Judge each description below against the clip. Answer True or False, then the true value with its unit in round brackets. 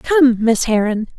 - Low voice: False (240 Hz)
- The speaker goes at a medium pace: True (150 wpm)